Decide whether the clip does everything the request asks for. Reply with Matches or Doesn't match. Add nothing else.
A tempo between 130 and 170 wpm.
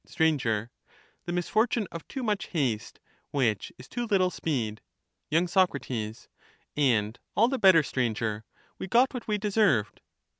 Matches